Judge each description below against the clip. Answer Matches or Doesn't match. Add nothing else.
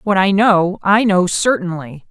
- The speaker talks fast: Doesn't match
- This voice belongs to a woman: Matches